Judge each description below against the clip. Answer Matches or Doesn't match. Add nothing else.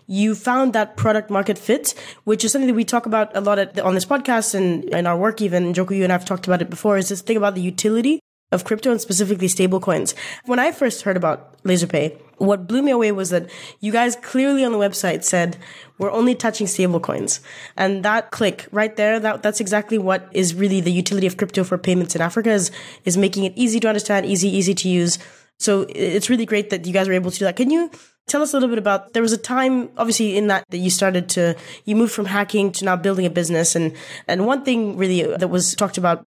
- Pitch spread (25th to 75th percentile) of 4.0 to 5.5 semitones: Doesn't match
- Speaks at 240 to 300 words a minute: Matches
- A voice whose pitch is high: Matches